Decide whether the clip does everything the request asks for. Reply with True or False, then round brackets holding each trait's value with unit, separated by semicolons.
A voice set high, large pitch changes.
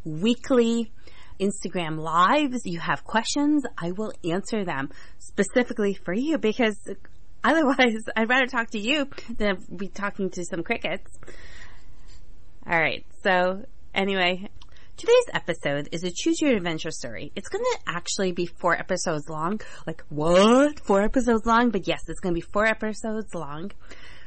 False (205 Hz; 5.0 semitones)